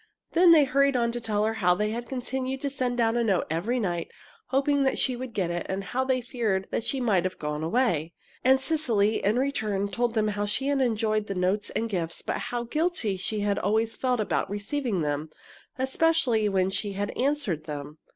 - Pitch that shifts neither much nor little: Yes, average, 4.9 semitones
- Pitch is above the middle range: Yes, high, 220 Hz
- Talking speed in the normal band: No, fast, 215 wpm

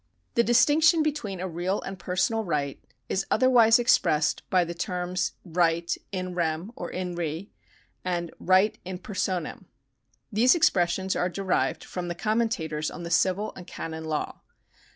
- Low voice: No, medium, 185 Hz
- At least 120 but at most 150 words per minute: No, average, 160 wpm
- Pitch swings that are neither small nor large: Yes, average, 3.7 semitones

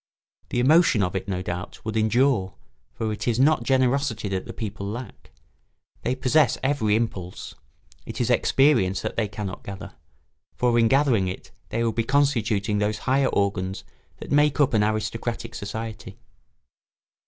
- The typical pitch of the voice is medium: No, low, 115 Hz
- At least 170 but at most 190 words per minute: No, average, 155 wpm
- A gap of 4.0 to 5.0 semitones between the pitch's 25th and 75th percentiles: Yes, average, 4.3 semitones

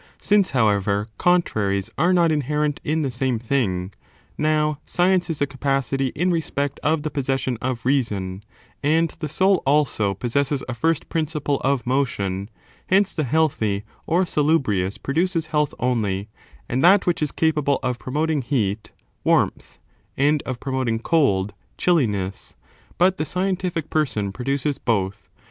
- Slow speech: No, average, 155 wpm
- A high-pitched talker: No, medium, 140 Hz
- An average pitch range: No, wide, 5.7 semitones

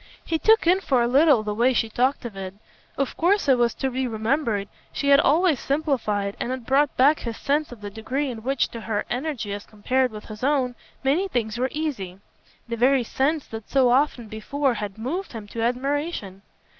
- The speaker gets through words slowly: No, fast, 205 wpm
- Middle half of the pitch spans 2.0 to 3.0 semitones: No, average, 4.4 semitones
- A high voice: Yes, very high, 255 Hz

